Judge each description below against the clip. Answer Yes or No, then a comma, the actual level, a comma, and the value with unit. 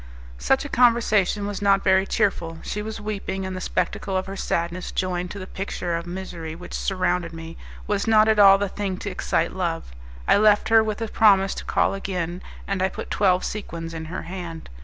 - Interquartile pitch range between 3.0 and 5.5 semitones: No, narrow, 2.6 semitones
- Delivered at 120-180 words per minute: No, fast, 205 wpm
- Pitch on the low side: No, high, 190 Hz